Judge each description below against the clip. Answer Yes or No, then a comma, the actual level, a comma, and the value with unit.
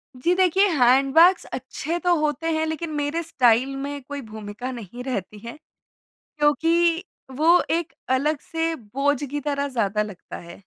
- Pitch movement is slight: No, average, 4.7 semitones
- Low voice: No, very high, 285 Hz